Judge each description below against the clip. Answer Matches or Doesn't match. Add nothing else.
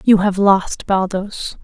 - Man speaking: Doesn't match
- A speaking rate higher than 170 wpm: Doesn't match